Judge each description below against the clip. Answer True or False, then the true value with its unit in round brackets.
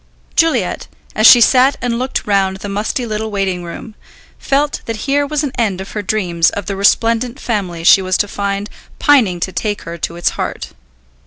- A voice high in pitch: True (210 Hz)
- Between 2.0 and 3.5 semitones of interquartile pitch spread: False (4.3 semitones)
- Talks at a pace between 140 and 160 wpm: False (190 wpm)